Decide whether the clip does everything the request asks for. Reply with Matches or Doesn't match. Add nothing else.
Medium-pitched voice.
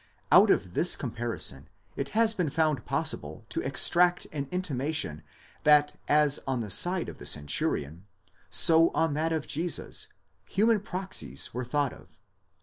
Matches